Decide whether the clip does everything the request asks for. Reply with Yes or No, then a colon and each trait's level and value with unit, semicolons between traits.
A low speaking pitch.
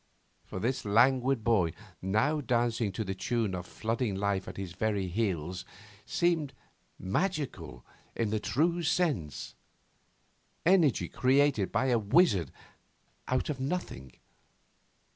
Yes: low, 115 Hz